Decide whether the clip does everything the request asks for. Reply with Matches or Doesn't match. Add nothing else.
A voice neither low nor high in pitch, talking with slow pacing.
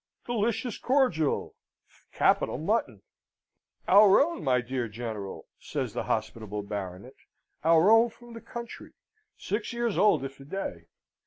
Matches